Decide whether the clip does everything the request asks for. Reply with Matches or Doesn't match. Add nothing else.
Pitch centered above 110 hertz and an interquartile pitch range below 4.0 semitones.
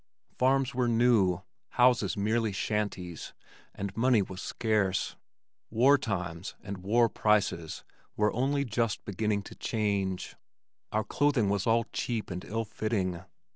Doesn't match